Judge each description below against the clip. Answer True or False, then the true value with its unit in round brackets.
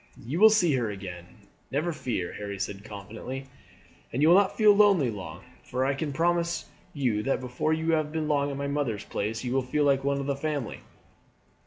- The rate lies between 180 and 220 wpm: True (205 wpm)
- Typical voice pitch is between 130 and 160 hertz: True (140 Hz)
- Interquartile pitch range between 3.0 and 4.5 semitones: False (5.6 semitones)